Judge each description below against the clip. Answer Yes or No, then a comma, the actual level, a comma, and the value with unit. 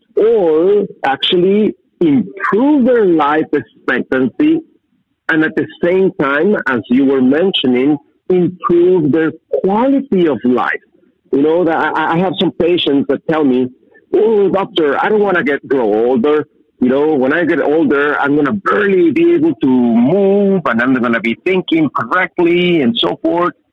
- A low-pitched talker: No, medium, 185 Hz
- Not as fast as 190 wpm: Yes, average, 155 wpm